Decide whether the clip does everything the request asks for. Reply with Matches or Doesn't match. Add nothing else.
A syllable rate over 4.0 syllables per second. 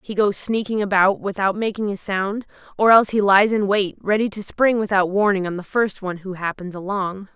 Matches